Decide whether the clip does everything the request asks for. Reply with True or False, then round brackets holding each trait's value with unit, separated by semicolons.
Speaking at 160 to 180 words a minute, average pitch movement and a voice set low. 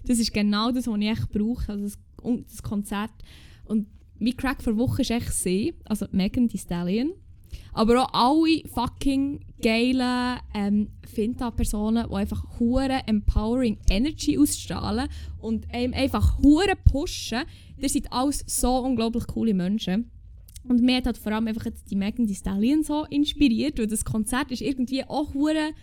False (165 wpm; 3.7 semitones; 235 Hz)